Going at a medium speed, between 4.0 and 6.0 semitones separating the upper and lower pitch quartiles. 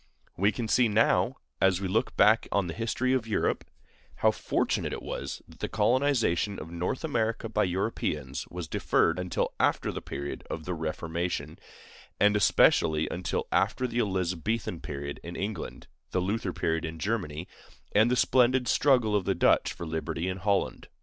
Yes: average, 170 wpm; average, 4.9 semitones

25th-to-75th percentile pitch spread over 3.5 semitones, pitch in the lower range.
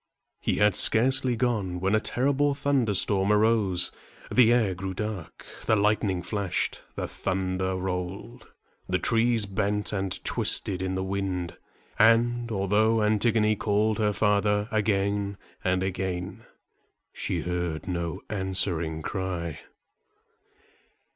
No: average, 2.9 semitones; low, 100 Hz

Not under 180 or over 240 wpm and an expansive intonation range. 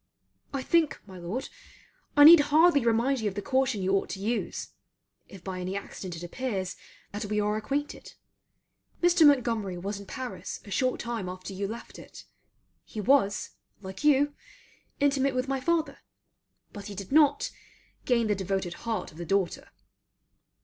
No: average, 165 wpm; wide, 5.9 semitones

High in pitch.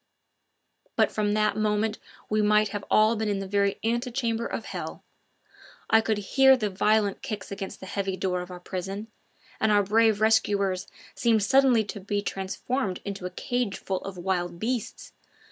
Yes: high, 210 Hz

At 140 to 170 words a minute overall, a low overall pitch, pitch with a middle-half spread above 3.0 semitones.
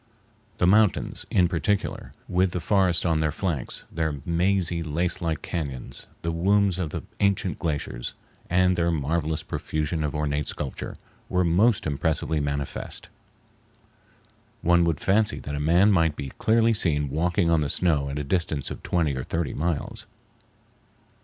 Yes: average, 150 wpm; very low, 85 Hz; average, 3.4 semitones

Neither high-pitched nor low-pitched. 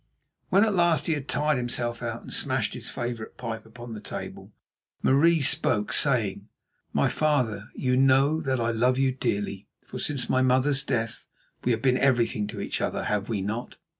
No: low, 125 Hz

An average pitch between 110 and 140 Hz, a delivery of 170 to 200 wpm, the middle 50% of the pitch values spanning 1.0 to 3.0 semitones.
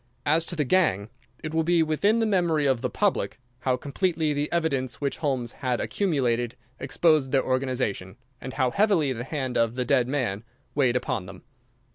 No: low, 135 Hz; average, 180 wpm; average, 4.4 semitones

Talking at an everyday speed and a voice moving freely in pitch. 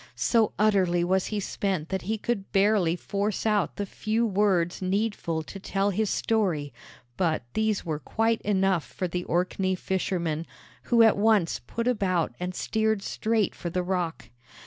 No: average, 160 wpm; average, 3.3 semitones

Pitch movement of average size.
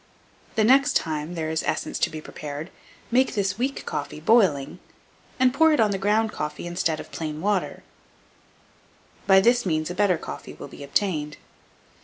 No: wide, 6.0 semitones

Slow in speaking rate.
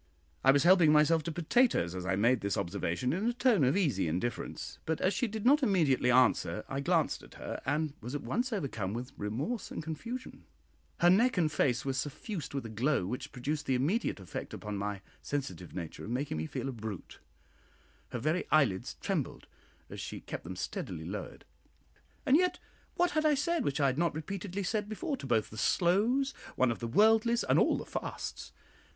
No: average, 200 wpm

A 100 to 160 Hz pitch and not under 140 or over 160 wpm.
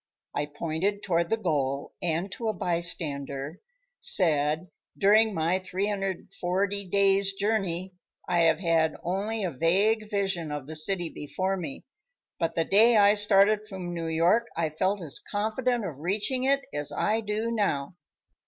No: medium, 185 Hz; average, 150 wpm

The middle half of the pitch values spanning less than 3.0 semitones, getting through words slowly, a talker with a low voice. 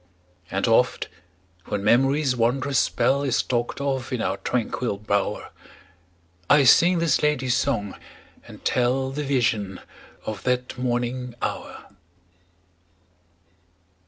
Yes: narrow, 2.6 semitones; slow, 110 wpm; low, 125 Hz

